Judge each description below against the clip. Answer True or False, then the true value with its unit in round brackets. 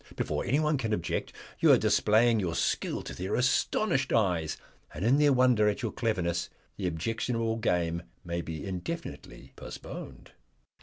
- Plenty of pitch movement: True (6.1 semitones)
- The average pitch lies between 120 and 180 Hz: False (110 Hz)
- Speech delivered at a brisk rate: False (150 wpm)